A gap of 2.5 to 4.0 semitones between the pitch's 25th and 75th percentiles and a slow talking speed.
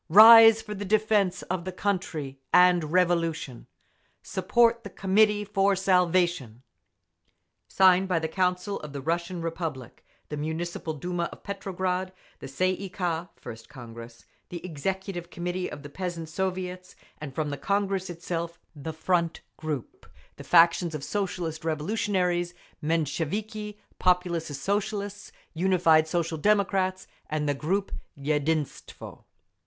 Yes: average, 3.3 semitones; slow, 125 wpm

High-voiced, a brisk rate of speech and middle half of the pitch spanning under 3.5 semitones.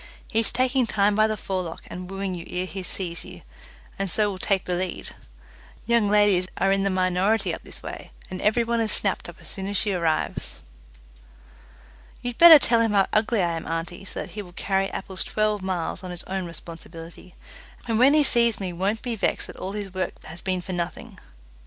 Yes: high, 195 Hz; fast, 215 wpm; average, 3.0 semitones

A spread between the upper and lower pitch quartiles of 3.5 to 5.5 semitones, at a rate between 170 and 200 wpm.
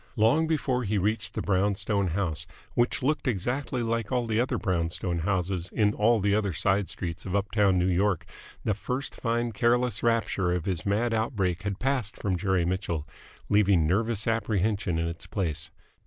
Yes: average, 3.9 semitones; average, 180 wpm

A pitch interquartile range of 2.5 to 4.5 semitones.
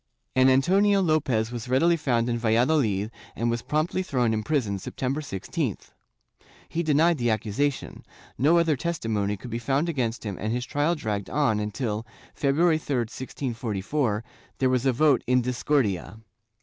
No: average, 5.0 semitones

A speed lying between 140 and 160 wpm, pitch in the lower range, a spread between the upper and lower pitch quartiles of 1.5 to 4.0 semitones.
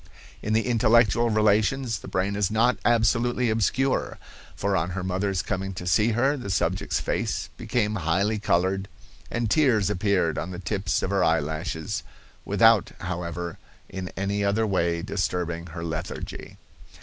Yes: average, 150 wpm; low, 100 Hz; average, 3.7 semitones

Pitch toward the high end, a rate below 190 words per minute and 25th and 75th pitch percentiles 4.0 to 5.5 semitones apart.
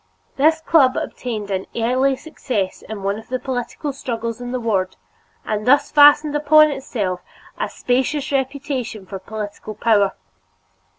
Yes: high, 245 Hz; average, 140 wpm; average, 4.7 semitones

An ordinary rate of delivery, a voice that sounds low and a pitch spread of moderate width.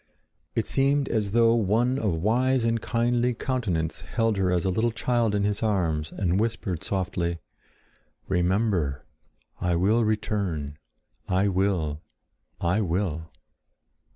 No: slow, 125 wpm; low, 100 Hz; average, 4.7 semitones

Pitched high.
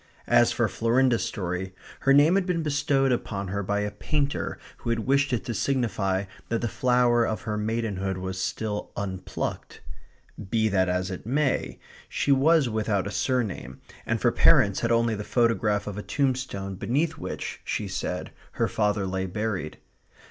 No: low, 110 Hz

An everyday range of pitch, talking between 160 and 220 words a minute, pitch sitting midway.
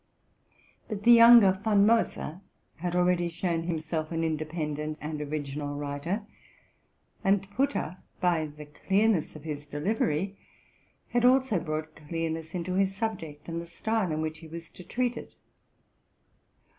No: average, 4.3 semitones; average, 140 wpm; medium, 170 Hz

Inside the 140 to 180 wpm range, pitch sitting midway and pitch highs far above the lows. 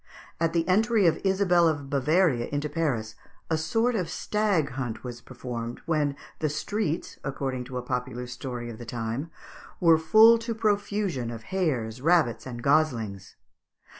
Yes: average, 155 wpm; medium, 145 Hz; wide, 6.4 semitones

